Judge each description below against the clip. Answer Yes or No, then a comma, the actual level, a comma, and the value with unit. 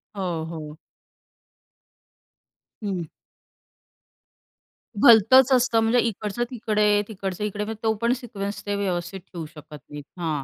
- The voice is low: No, high, 205 Hz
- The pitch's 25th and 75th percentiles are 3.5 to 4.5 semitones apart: Yes, average, 4.2 semitones